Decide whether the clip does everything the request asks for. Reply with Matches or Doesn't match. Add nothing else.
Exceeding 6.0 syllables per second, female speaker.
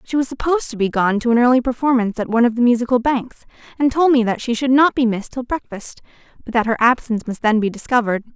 Matches